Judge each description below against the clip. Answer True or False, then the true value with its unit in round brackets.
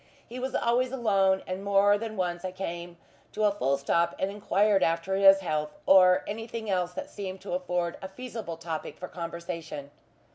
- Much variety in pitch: False (3.1 semitones)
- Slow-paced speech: False (180 wpm)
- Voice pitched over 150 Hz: True (190 Hz)